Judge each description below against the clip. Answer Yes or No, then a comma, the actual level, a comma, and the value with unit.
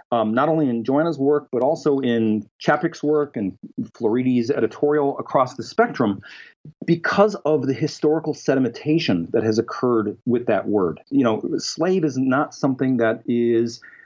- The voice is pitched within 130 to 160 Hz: Yes, medium, 140 Hz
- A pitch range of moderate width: Yes, average, 4.3 semitones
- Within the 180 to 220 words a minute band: No, average, 155 wpm